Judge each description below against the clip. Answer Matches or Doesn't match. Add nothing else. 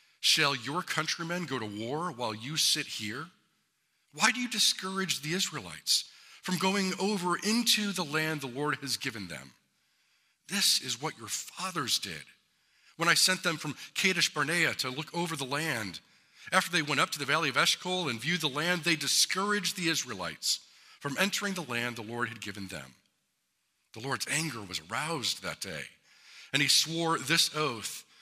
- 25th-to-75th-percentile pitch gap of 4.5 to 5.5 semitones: Matches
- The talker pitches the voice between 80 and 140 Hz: Doesn't match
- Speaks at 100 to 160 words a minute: Doesn't match